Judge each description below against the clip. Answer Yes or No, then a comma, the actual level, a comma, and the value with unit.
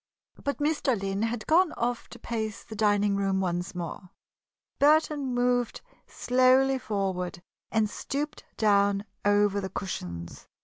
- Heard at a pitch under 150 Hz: No, high, 215 Hz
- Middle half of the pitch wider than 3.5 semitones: Yes, average, 4.6 semitones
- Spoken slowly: Yes, slow, 130 wpm